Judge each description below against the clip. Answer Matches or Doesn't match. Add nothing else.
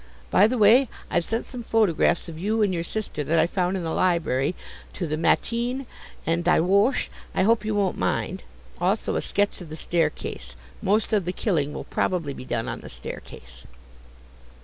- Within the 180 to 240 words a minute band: Matches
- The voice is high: Doesn't match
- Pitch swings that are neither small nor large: Matches